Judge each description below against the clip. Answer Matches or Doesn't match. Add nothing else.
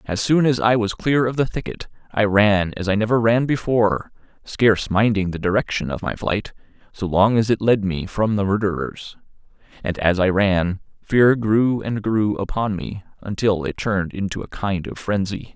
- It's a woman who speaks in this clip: Doesn't match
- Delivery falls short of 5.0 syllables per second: Matches